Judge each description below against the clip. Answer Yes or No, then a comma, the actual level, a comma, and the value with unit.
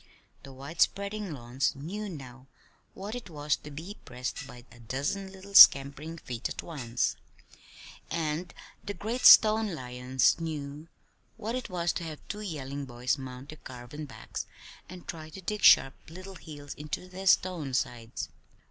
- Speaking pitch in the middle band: Yes, medium, 150 Hz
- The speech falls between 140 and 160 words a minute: Yes, average, 155 wpm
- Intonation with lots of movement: Yes, wide, 5.9 semitones